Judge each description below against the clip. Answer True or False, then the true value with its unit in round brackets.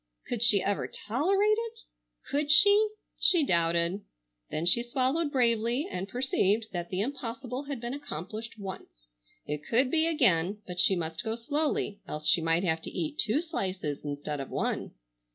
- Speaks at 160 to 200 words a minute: True (165 wpm)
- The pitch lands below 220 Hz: False (230 Hz)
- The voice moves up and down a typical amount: False (8.2 semitones)